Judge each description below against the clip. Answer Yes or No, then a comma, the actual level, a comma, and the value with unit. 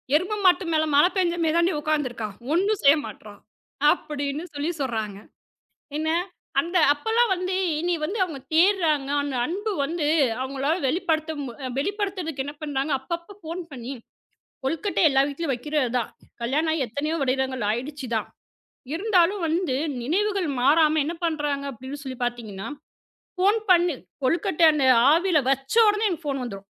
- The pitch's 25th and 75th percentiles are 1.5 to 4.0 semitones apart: No, average, 4.6 semitones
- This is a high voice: Yes, very high, 310 Hz